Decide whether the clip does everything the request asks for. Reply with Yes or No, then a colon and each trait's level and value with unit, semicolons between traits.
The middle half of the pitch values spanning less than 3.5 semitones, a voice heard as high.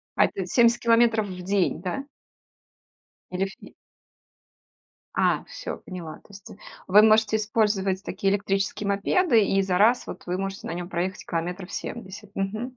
Yes: narrow, 2.6 semitones; high, 200 Hz